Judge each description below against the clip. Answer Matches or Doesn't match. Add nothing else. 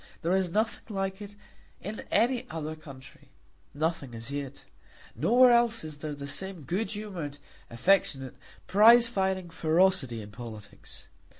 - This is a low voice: Doesn't match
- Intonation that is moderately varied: Doesn't match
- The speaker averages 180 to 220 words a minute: Doesn't match